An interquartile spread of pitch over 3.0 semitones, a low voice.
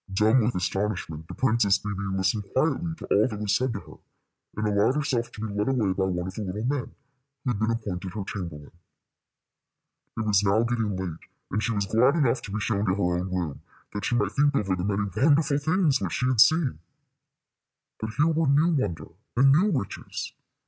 Yes: average, 5.2 semitones; low, 110 Hz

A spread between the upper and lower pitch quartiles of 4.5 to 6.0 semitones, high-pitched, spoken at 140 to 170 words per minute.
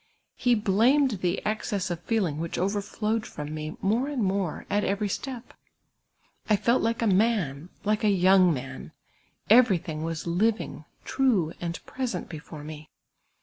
Yes: average, 5.2 semitones; high, 195 Hz; average, 150 wpm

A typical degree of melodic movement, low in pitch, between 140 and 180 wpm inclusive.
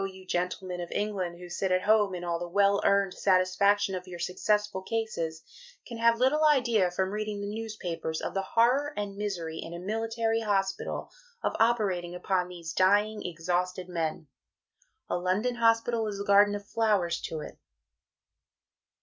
No: average, 3.3 semitones; high, 195 Hz; average, 165 wpm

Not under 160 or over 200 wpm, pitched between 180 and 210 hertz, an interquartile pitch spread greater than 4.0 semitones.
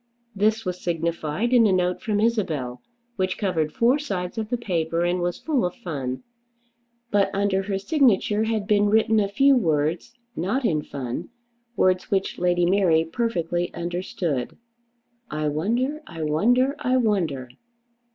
No: average, 150 wpm; medium, 185 Hz; average, 5.0 semitones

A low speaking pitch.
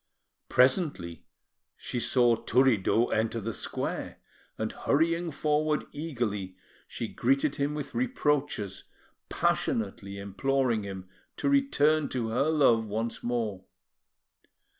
Yes: low, 125 Hz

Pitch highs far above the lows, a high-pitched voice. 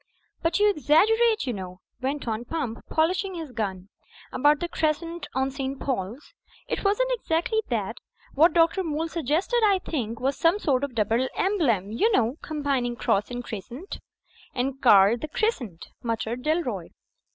Yes: wide, 6.2 semitones; very high, 280 Hz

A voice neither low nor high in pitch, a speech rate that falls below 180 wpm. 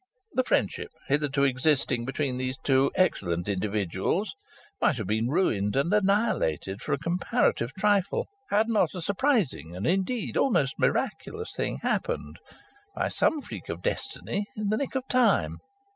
Yes: medium, 150 Hz; average, 155 wpm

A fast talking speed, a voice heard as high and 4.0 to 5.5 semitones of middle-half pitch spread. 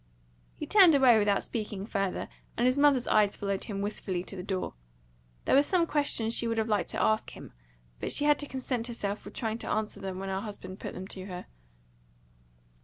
Yes: fast, 215 wpm; high, 215 Hz; average, 4.3 semitones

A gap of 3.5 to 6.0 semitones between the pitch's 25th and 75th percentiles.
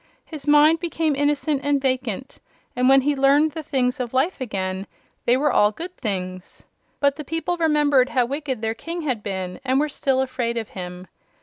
Yes: average, 4.1 semitones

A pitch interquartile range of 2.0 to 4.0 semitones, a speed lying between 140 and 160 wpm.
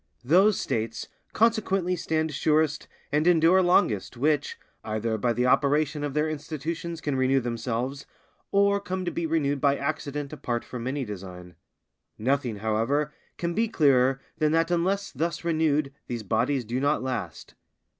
No: average, 4.9 semitones; average, 150 wpm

